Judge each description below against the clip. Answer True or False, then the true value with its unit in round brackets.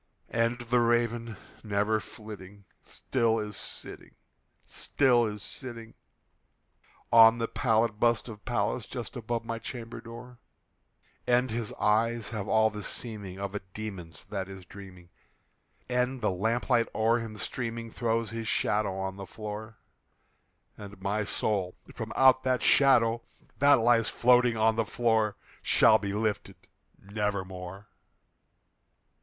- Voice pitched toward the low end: True (110 Hz)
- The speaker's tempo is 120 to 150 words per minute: True (135 wpm)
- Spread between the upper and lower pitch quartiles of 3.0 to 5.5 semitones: False (2.4 semitones)